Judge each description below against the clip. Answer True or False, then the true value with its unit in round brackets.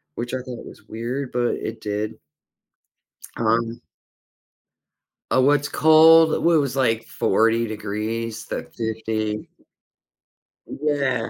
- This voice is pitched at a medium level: False (115 Hz)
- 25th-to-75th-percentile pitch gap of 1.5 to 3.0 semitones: False (3.7 semitones)